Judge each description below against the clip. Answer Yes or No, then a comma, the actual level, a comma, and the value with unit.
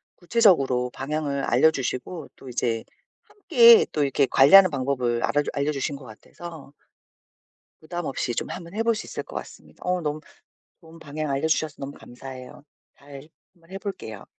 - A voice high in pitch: No, medium, 145 Hz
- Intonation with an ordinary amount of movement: Yes, average, 4.3 semitones